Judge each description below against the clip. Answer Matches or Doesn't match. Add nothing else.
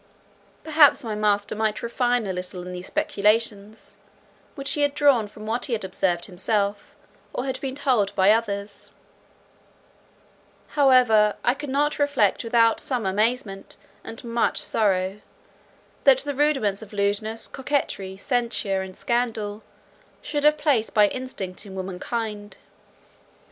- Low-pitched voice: Doesn't match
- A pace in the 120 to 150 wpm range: Matches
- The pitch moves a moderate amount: Matches